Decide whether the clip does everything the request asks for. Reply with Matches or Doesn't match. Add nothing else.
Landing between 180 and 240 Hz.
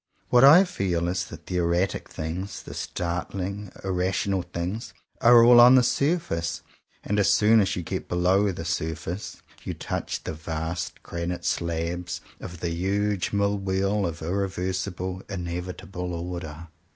Doesn't match